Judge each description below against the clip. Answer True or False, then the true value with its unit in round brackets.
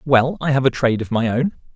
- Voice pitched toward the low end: True (130 Hz)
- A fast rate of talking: True (275 wpm)